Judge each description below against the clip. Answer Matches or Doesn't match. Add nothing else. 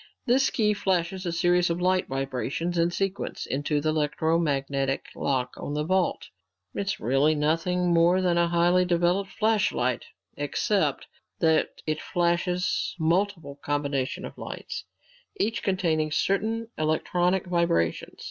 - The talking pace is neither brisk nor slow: Doesn't match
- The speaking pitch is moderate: Matches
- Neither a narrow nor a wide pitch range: Matches